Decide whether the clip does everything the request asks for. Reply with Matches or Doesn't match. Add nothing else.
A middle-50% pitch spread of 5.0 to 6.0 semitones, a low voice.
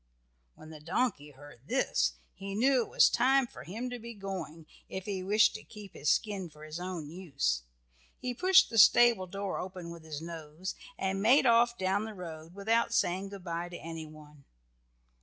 Doesn't match